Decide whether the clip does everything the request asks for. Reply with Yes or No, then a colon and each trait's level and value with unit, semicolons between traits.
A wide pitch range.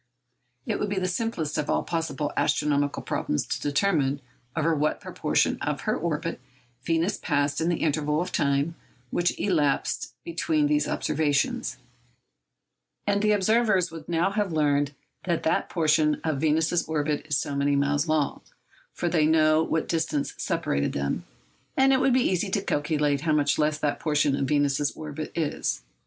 No: average, 2.8 semitones